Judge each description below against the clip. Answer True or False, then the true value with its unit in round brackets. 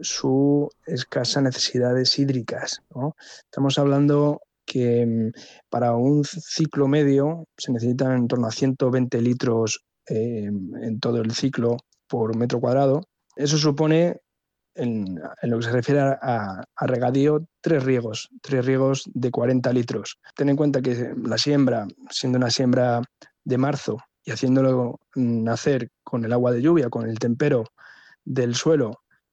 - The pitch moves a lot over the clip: False (2.9 semitones)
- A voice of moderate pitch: False (130 Hz)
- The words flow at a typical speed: True (140 wpm)